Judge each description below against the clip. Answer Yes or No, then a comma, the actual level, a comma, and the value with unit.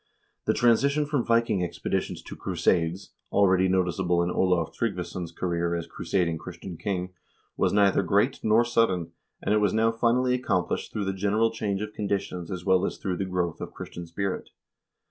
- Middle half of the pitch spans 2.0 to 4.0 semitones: Yes, average, 3.7 semitones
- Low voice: Yes, very low, 95 Hz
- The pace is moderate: Yes, average, 170 wpm